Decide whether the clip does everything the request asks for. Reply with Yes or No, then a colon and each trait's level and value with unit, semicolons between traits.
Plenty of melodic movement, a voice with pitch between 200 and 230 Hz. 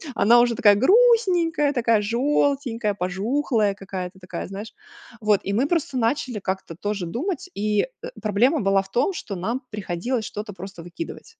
Yes: wide, 5.7 semitones; high, 215 Hz